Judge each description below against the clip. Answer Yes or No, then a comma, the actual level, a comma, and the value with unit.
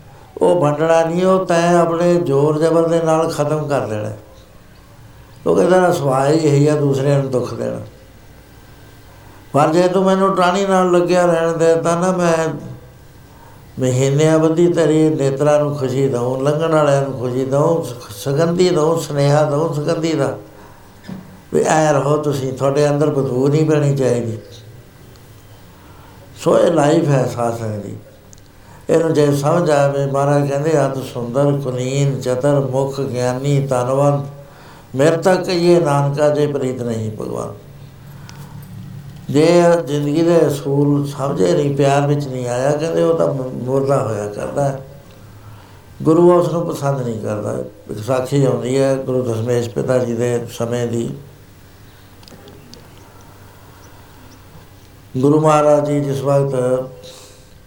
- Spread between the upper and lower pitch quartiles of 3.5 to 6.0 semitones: Yes, average, 4.2 semitones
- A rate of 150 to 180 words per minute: No, average, 130 wpm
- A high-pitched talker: No, low, 135 Hz